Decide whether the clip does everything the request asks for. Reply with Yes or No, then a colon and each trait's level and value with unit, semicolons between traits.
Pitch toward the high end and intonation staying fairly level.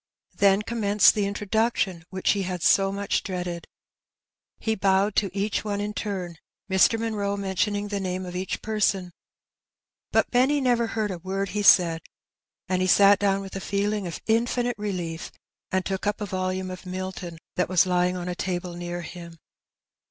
Yes: high, 195 Hz; narrow, 2.2 semitones